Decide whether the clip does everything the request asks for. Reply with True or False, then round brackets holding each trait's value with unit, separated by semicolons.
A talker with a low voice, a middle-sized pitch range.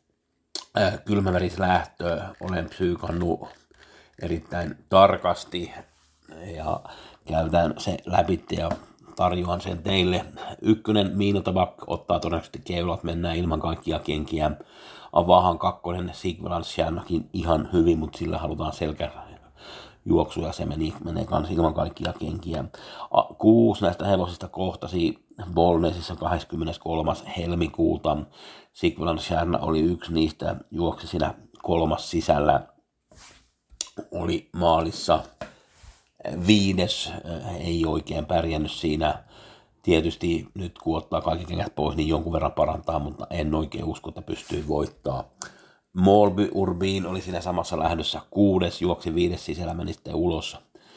False (85 Hz; 2.3 semitones)